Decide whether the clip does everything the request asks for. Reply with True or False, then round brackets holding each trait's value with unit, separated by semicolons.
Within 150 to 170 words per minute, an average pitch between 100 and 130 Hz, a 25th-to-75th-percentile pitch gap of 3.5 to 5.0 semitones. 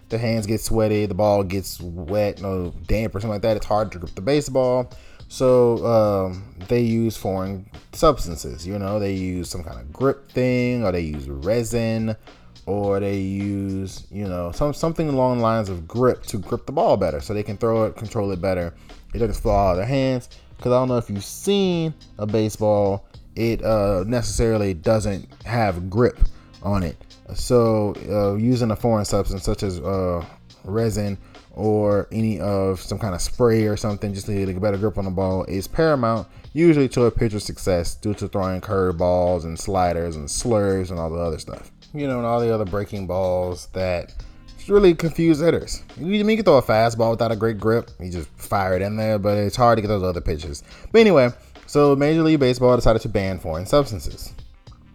False (205 wpm; 105 Hz; 3.9 semitones)